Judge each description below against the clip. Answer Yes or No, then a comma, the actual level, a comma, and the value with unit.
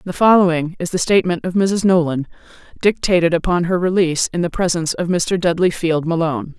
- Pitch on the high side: No, medium, 175 Hz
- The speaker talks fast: No, average, 180 wpm